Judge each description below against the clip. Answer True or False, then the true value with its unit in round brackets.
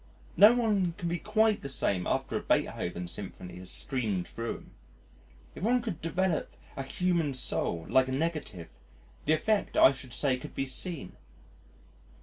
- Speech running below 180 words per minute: True (160 wpm)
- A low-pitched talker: False (145 Hz)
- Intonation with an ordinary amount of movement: False (8.1 semitones)